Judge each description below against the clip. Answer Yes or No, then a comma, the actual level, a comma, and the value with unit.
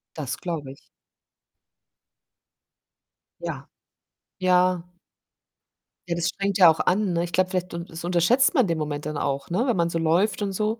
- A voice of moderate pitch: Yes, medium, 175 Hz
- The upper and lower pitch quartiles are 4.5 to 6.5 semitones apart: No, average, 2.8 semitones